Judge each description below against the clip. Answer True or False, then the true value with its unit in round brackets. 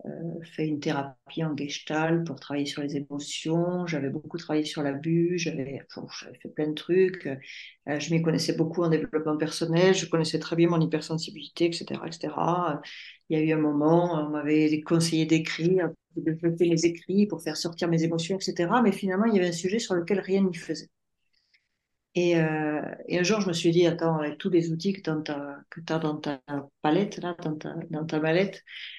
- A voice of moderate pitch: True (160 Hz)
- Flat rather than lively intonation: True (2.2 semitones)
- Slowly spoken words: False (205 wpm)